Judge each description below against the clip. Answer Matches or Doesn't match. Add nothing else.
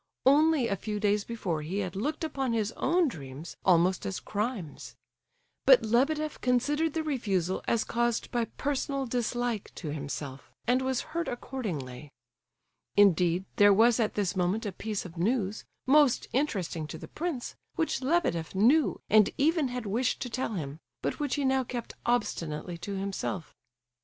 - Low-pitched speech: Doesn't match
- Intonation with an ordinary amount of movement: Doesn't match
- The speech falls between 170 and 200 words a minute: Doesn't match